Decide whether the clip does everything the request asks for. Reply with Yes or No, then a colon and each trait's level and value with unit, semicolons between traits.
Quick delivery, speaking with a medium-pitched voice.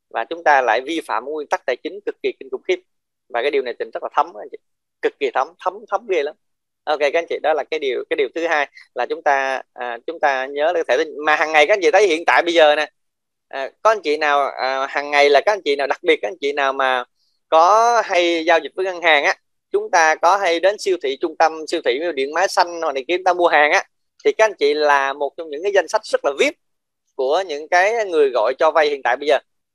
Yes: fast, 280 wpm; medium, 175 Hz